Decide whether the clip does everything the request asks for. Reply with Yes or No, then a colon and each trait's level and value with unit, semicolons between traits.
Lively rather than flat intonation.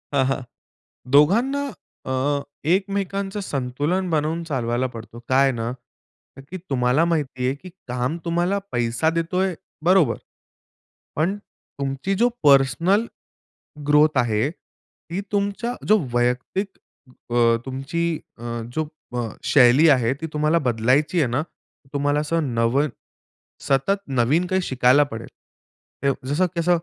Yes: wide, 5.8 semitones